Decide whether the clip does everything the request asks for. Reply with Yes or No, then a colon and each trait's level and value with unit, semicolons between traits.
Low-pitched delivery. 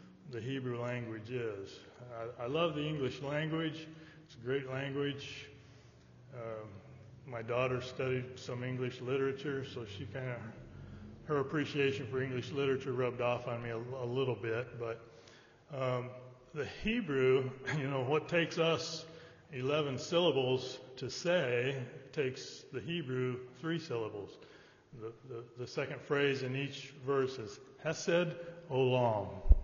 Yes: low, 130 Hz